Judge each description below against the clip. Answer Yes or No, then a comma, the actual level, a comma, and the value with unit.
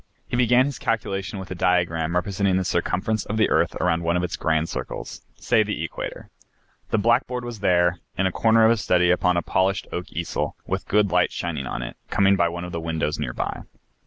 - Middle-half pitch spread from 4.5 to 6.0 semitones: No, average, 3.6 semitones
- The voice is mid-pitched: No, very low, 90 Hz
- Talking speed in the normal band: No, fast, 220 wpm